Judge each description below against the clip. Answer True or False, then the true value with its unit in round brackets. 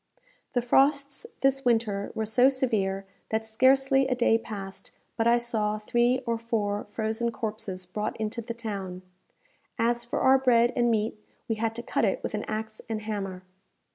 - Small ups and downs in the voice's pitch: True (2.3 semitones)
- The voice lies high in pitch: True (225 Hz)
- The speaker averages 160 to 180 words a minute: True (170 wpm)